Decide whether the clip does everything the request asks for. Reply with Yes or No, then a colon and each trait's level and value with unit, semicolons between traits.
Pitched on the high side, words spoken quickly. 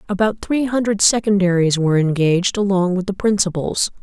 No: high, 195 Hz; average, 150 wpm